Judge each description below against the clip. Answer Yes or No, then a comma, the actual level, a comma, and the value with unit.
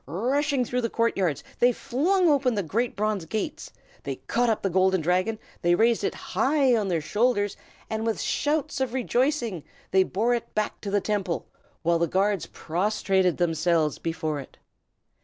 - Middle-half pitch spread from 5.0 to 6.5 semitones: Yes, average, 5.3 semitones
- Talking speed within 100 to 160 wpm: No, average, 175 wpm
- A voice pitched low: No, high, 210 Hz